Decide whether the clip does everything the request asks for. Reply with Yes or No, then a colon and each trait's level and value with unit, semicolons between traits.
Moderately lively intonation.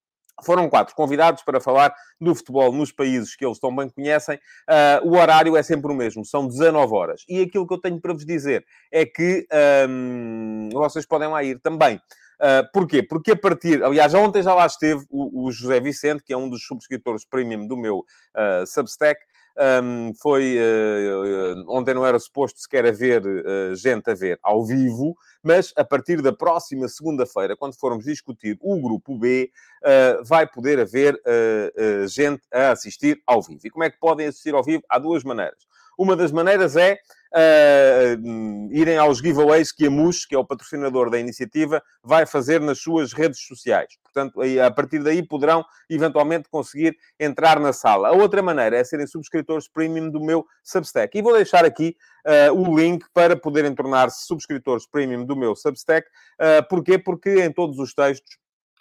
Yes: average, 4.1 semitones